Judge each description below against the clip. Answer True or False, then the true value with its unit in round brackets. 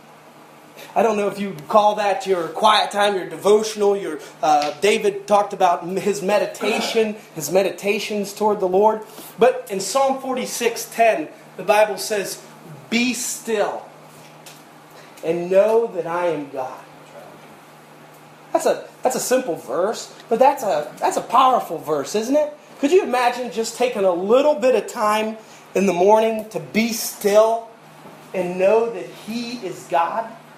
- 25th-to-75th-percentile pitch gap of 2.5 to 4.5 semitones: True (3.4 semitones)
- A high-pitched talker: True (210 Hz)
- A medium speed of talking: True (150 wpm)